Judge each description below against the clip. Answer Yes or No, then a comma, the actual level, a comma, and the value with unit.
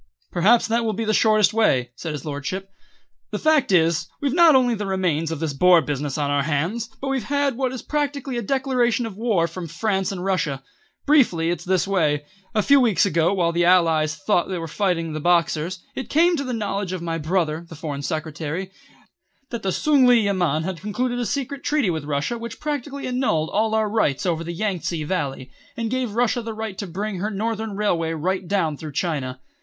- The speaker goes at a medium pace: No, fast, 210 wpm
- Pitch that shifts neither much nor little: No, wide, 6.2 semitones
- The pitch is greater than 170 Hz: Yes, high, 190 Hz